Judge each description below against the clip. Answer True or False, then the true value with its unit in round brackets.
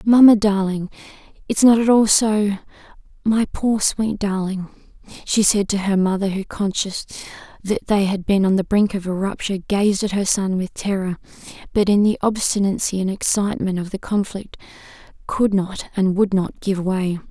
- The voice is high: True (200 Hz)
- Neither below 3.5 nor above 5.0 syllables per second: True (4.9 syllables/s)